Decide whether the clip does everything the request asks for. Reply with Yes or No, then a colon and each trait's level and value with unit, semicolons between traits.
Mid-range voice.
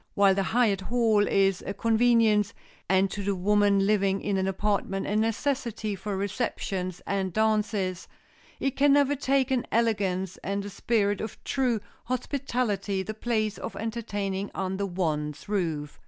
No: high, 205 Hz